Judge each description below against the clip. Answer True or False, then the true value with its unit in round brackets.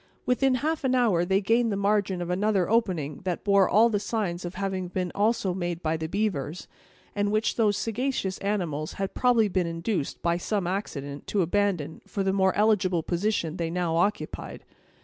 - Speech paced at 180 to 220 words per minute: True (185 wpm)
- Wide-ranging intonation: False (3.5 semitones)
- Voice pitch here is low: False (195 Hz)